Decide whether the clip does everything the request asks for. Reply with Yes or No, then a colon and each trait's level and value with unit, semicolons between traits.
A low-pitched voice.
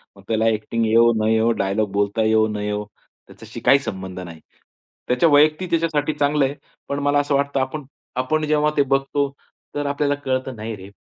Yes: low, 130 Hz